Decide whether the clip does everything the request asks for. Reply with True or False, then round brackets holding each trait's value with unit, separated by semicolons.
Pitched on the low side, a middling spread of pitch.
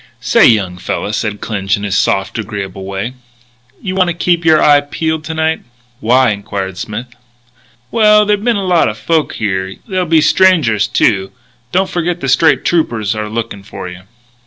False (120 Hz; 8.6 semitones)